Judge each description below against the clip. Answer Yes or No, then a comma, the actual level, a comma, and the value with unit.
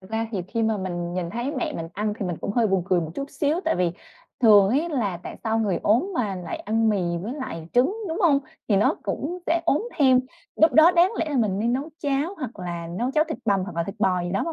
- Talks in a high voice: Yes, high, 225 Hz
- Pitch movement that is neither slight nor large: No, wide, 6.9 semitones